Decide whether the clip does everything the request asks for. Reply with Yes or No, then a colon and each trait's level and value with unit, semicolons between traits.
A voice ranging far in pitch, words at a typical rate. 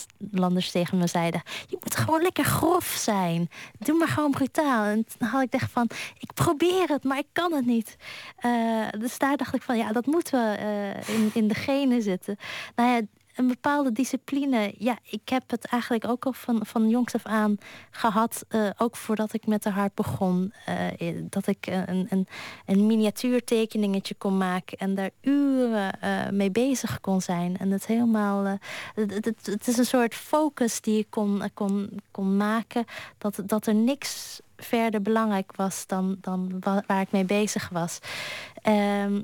No: average, 3.7 semitones; average, 180 wpm